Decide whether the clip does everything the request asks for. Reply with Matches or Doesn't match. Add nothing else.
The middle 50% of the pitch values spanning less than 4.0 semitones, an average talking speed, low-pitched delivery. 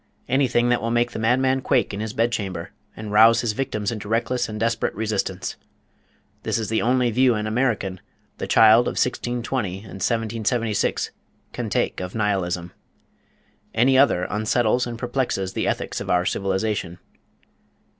Matches